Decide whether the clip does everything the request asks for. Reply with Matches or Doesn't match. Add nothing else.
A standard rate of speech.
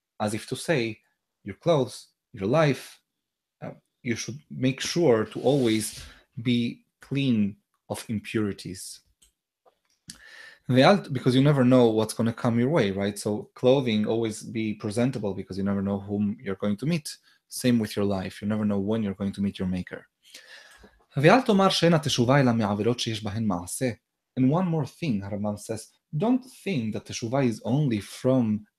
Matches